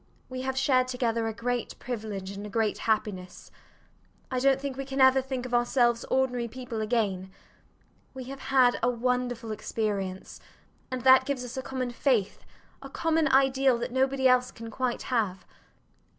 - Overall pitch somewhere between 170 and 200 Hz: No, very high, 250 Hz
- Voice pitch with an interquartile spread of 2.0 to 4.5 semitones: Yes, average, 2.7 semitones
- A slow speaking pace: No, average, 165 wpm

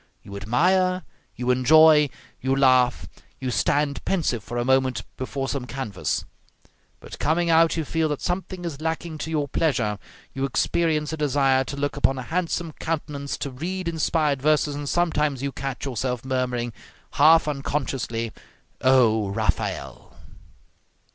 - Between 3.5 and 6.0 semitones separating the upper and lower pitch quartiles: Yes, average, 3.8 semitones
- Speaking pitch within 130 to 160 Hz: Yes, medium, 140 Hz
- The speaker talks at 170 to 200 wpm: No, average, 145 wpm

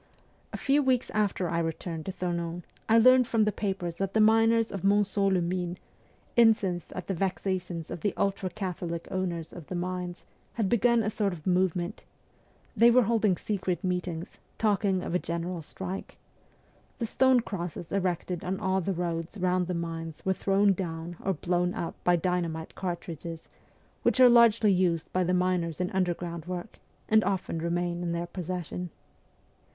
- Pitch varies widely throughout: No, narrow, 2.6 semitones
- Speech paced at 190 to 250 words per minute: No, average, 170 wpm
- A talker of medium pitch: Yes, medium, 180 Hz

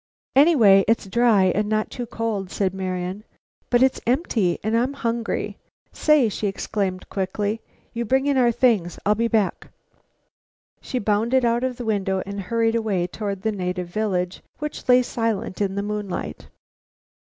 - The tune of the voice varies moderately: Yes, average, 3.5 semitones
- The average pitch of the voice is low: No, high, 215 Hz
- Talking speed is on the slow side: No, average, 160 wpm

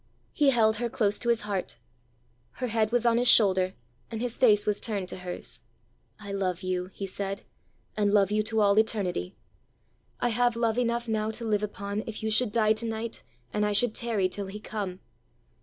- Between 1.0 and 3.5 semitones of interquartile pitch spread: Yes, narrow, 2.4 semitones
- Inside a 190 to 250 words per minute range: Yes, average, 200 wpm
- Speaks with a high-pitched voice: Yes, high, 215 Hz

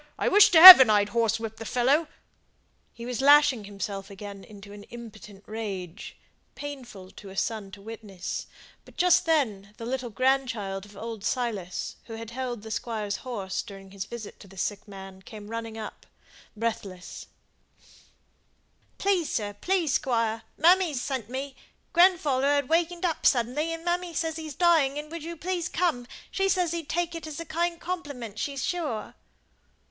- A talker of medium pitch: No, high, 240 Hz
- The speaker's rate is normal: Yes, average, 165 wpm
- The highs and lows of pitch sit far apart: Yes, wide, 7.4 semitones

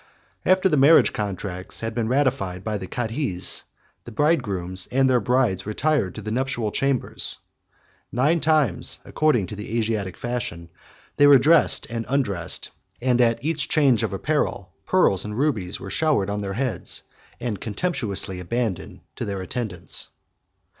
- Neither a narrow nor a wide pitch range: No, wide, 5.8 semitones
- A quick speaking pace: No, average, 155 wpm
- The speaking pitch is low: Yes, low, 115 Hz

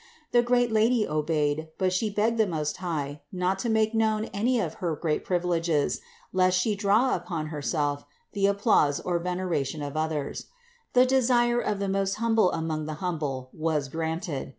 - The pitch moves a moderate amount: No, wide, 5.7 semitones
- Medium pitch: Yes, medium, 180 Hz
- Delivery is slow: No, average, 175 wpm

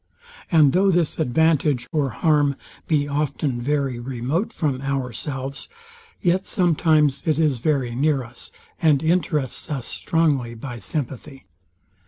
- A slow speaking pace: Yes, slow, 125 wpm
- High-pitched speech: No, medium, 145 Hz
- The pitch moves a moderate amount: Yes, average, 3.3 semitones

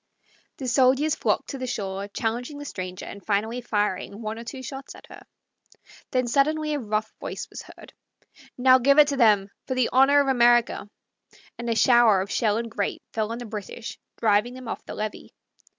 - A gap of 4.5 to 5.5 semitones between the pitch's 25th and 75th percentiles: No, average, 3.5 semitones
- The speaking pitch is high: Yes, high, 235 Hz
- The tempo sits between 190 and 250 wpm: Yes, average, 195 wpm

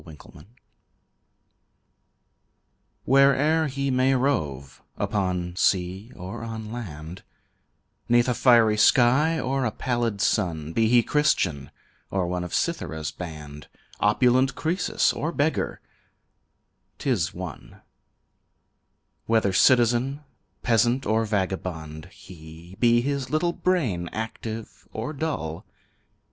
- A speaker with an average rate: No, slow, 105 wpm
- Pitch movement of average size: No, wide, 6.7 semitones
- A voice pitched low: Yes, low, 115 Hz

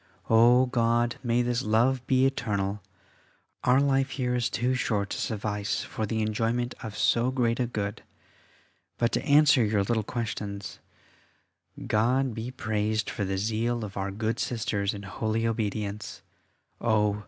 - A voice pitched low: Yes, low, 115 Hz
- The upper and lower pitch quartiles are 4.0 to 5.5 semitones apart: No, average, 2.7 semitones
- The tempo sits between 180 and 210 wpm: No, average, 150 wpm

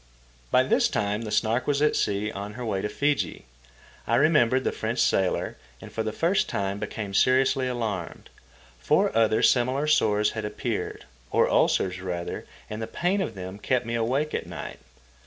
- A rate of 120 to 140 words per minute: No, average, 175 wpm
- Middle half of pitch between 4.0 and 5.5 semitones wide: Yes, average, 4.3 semitones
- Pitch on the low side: Yes, low, 110 Hz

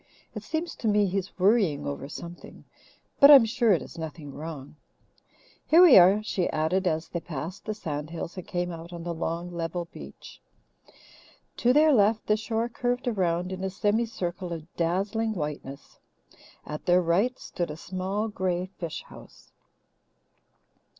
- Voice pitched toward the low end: No, medium, 180 Hz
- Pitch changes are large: No, average, 4.4 semitones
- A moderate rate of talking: Yes, average, 165 wpm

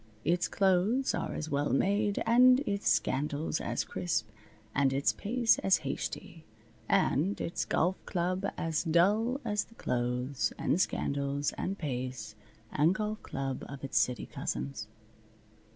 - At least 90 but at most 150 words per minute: Yes, slow, 135 wpm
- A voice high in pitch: No, medium, 165 Hz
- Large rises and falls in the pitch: Yes, wide, 6.7 semitones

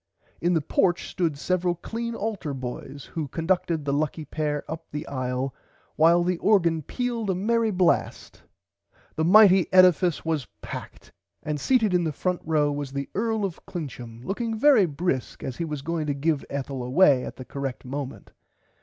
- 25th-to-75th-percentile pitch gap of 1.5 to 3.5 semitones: No, average, 4.7 semitones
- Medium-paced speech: Yes, average, 170 wpm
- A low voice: No, medium, 165 Hz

